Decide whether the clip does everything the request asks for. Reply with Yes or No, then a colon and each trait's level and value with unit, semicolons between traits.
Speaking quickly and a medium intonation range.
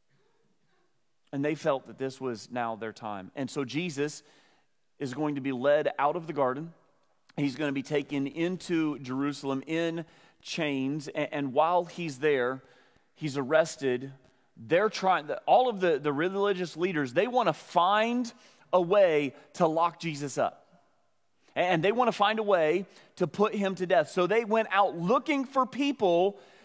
No: average, 170 wpm; average, 5.0 semitones